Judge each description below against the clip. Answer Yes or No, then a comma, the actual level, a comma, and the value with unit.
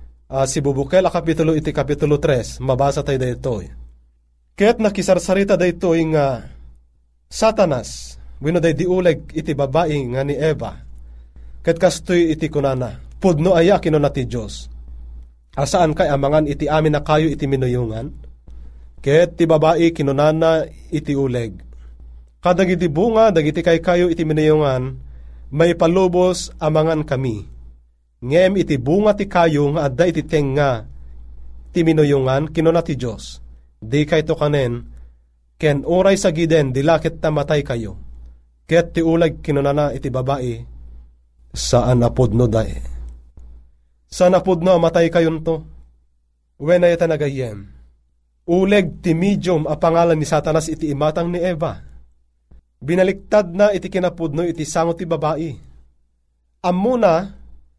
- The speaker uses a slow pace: No, average, 125 wpm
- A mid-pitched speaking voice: Yes, medium, 145 Hz